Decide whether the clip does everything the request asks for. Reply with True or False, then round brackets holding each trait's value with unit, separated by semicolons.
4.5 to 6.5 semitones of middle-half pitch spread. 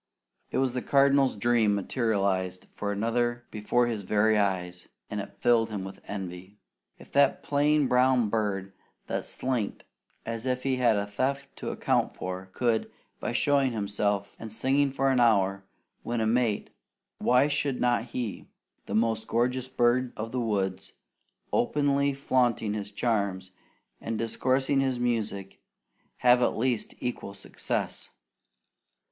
False (3.9 semitones)